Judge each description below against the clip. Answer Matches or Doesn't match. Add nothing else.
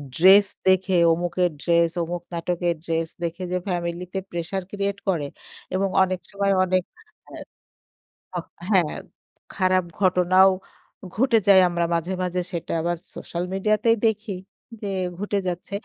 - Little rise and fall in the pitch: Matches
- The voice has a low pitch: Doesn't match